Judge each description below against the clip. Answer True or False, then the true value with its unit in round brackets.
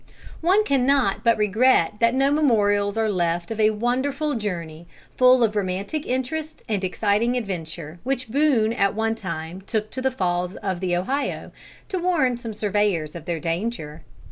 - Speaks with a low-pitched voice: False (215 Hz)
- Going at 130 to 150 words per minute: False (165 wpm)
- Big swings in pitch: True (5.7 semitones)